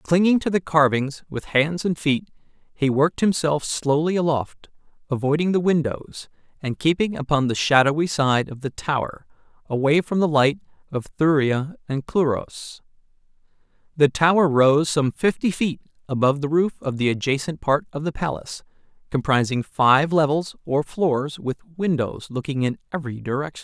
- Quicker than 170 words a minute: No, average, 150 wpm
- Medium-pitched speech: Yes, medium, 150 Hz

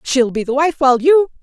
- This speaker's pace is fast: Yes, fast, 255 wpm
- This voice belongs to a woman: Yes, female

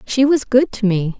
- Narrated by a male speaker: No, female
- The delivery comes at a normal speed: No, fast, 250 wpm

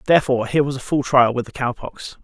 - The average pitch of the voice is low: Yes, low, 130 Hz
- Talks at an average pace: No, fast, 270 wpm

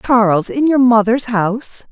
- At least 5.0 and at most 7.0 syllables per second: No, 4.6 syllables/s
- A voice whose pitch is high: Yes, high, 230 Hz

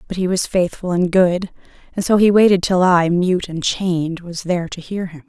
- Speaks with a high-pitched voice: No, medium, 180 Hz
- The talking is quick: Yes, fast, 225 wpm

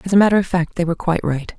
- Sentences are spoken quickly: Yes, fast, 340 wpm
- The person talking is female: Yes, female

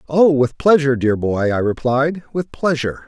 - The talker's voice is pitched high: No, low, 135 Hz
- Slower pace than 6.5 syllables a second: Yes, 5.0 syllables/s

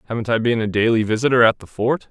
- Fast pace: Yes, fast, 255 wpm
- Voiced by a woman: No, male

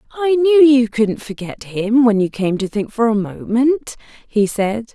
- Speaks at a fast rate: No, average, 195 wpm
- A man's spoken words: No, female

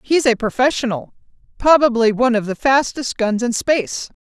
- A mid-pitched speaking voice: No, high, 240 Hz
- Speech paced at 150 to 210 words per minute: No, average, 140 wpm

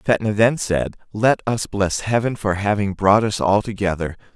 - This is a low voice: Yes, low, 100 Hz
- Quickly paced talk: No, average, 180 wpm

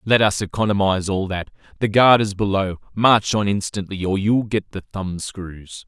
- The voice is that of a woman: No, male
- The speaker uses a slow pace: No, average, 185 wpm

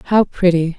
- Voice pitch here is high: No, medium, 180 Hz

